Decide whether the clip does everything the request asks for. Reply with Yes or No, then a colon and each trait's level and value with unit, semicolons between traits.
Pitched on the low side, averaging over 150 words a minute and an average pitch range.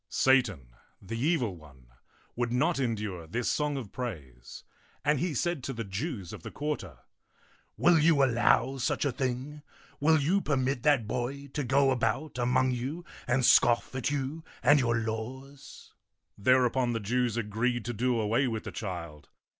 Yes: low, 125 Hz; average, 170 wpm; average, 3.9 semitones